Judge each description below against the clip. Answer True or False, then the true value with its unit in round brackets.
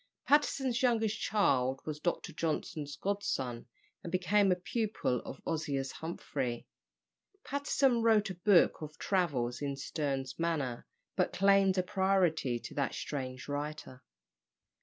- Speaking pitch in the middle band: True (165 Hz)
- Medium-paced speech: False (125 wpm)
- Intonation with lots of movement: True (6.5 semitones)